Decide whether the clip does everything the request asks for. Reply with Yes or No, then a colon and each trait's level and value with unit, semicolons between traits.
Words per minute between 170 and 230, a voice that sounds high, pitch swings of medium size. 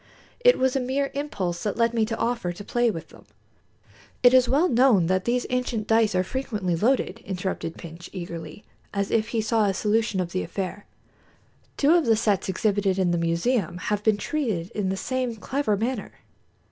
Yes: average, 190 wpm; high, 215 Hz; average, 4.9 semitones